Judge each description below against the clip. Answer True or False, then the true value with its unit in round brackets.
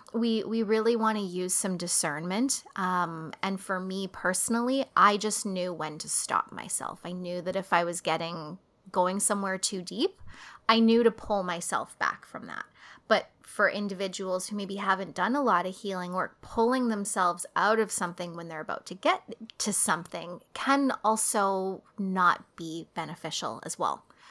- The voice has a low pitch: False (190 Hz)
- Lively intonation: False (3.5 semitones)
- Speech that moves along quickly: False (175 wpm)